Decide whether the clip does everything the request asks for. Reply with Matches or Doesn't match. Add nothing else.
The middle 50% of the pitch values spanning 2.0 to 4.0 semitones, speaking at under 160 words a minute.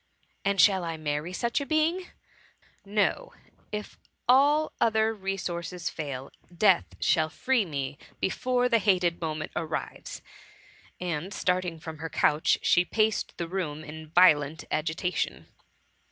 Doesn't match